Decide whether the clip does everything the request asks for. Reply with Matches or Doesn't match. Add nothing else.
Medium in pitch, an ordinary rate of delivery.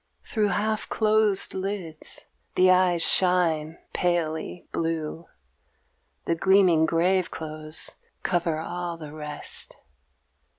Doesn't match